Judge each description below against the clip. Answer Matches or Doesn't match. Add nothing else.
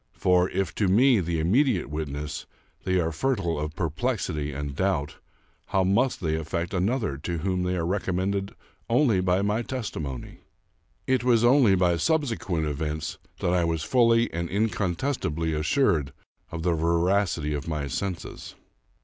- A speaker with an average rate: Matches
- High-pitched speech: Doesn't match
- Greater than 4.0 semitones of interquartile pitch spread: Matches